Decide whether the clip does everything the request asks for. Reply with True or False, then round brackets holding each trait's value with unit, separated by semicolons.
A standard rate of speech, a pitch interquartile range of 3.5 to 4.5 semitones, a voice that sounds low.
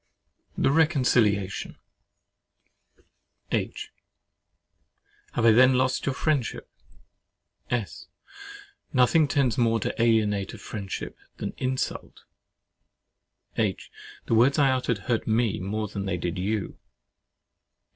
False (100 wpm; 4.0 semitones; 115 Hz)